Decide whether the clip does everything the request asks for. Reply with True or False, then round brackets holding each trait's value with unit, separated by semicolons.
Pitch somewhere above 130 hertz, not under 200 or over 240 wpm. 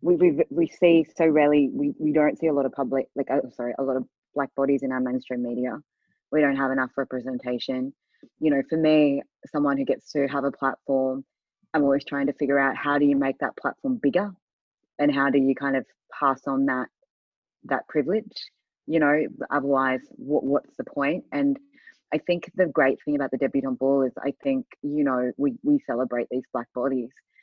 True (140 Hz; 205 wpm)